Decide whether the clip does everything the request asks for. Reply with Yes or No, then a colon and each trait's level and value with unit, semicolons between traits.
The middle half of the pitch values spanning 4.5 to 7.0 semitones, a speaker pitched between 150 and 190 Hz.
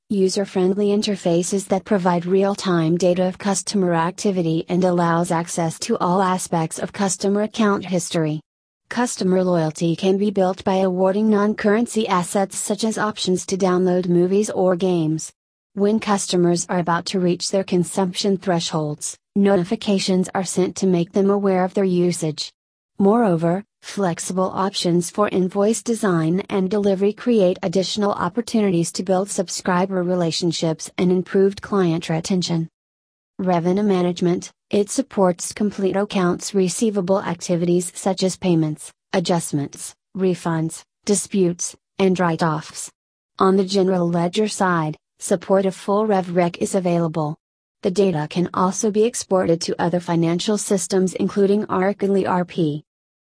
No: narrow, 2.5 semitones; medium, 185 Hz